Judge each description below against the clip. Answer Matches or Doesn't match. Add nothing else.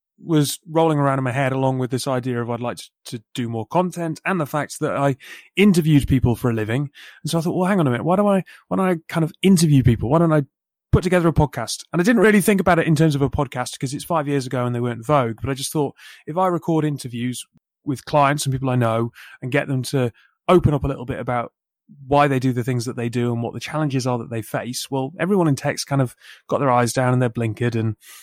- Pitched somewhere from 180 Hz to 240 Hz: Doesn't match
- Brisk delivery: Matches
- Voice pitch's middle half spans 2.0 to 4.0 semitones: Doesn't match